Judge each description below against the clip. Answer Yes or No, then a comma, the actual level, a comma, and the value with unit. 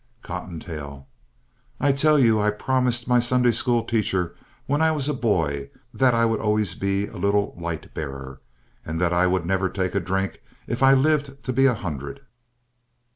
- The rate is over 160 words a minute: Yes, average, 180 wpm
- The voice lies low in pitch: Yes, low, 105 Hz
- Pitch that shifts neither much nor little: No, wide, 6.3 semitones